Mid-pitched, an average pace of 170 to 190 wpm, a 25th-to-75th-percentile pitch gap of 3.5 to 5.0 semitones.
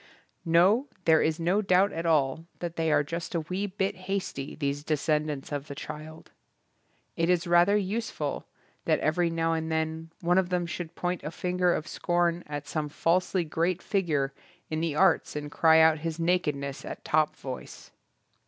No: medium, 165 Hz; average, 175 wpm; average, 2.7 semitones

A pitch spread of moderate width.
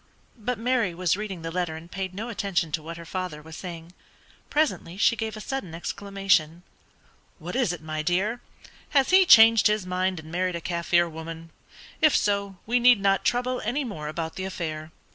Yes: average, 4.8 semitones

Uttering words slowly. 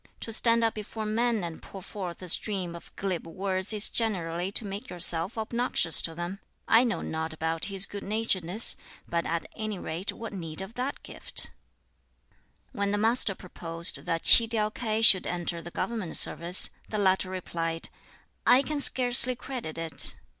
No: average, 170 wpm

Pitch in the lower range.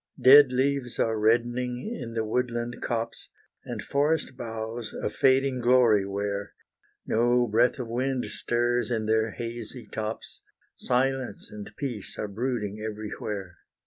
Yes: low, 120 Hz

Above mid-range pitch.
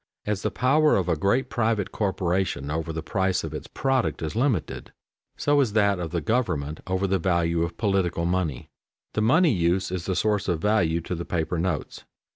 No: very low, 95 Hz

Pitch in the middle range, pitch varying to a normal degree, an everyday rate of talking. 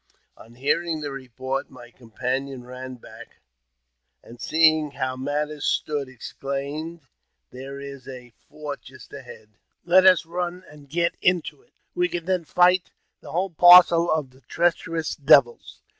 Yes: medium, 145 Hz; average, 4.6 semitones; average, 145 wpm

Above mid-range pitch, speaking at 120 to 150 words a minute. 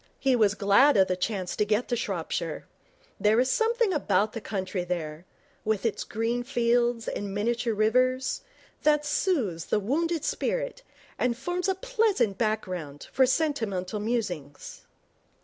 Yes: high, 230 Hz; average, 145 wpm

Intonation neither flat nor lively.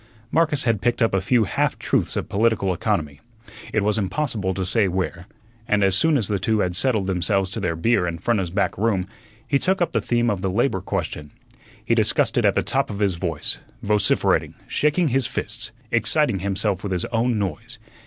Yes: average, 3.9 semitones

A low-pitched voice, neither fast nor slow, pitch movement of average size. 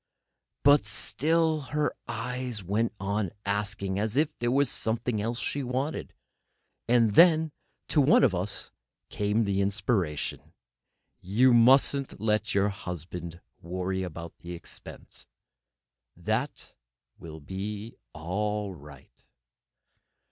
No: low, 105 Hz; slow, 110 wpm; average, 4.9 semitones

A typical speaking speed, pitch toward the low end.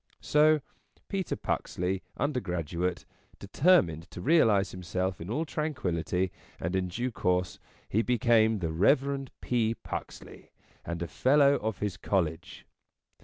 No: slow, 120 wpm; low, 100 Hz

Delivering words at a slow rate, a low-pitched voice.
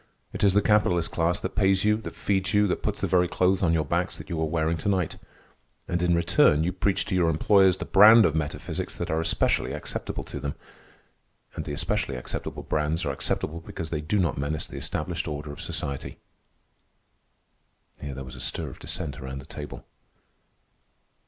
No: average, 195 wpm; very low, 85 Hz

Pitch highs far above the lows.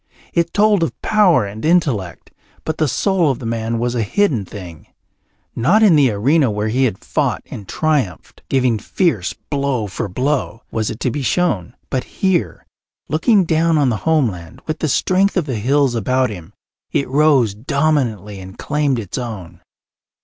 Yes: wide, 6.5 semitones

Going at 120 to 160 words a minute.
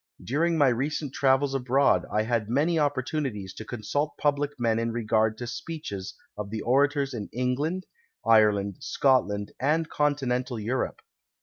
Yes: average, 140 wpm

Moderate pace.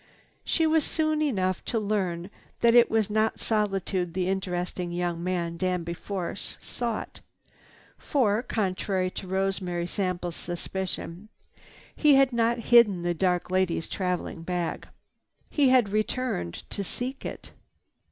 No: slow, 130 wpm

